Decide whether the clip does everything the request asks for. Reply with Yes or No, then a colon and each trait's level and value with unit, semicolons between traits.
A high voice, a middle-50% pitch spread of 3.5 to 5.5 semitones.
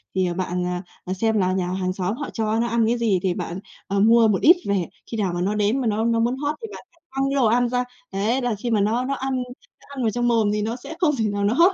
Yes: high, 225 Hz; average, 4.0 semitones